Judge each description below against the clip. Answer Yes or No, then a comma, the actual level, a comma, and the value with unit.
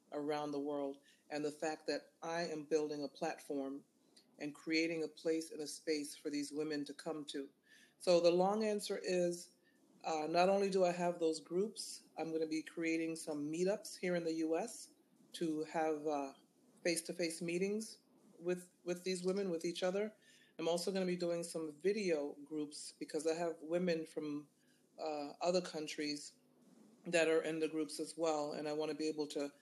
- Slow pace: No, average, 190 wpm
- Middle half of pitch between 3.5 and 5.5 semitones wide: No, average, 2.8 semitones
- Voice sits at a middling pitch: Yes, medium, 160 Hz